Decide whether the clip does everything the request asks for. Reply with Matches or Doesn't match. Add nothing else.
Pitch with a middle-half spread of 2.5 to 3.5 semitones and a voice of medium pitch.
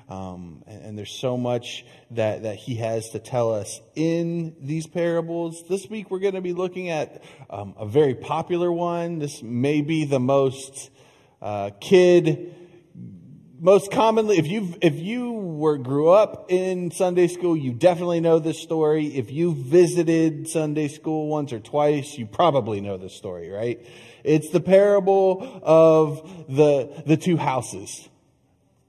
Doesn't match